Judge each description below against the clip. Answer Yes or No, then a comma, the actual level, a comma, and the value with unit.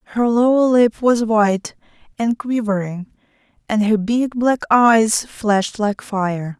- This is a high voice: Yes, high, 220 Hz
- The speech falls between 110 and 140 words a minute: Yes, slow, 135 wpm